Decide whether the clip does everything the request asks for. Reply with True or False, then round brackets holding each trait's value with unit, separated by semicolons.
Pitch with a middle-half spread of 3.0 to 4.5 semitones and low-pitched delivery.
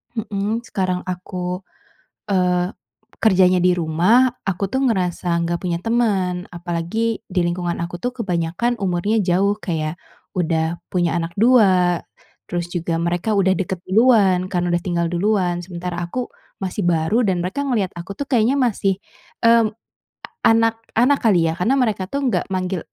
False (4.0 semitones; 185 Hz)